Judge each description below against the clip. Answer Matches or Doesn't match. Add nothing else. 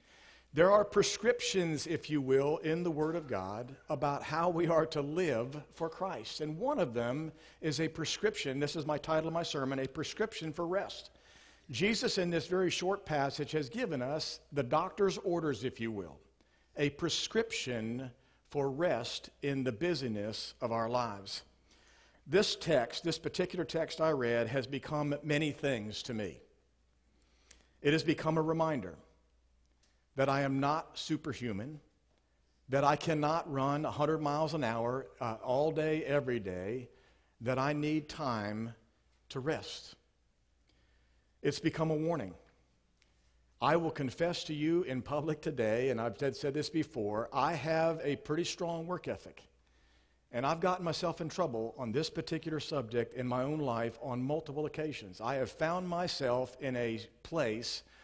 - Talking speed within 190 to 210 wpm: Doesn't match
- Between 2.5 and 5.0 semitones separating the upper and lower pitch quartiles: Doesn't match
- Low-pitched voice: Doesn't match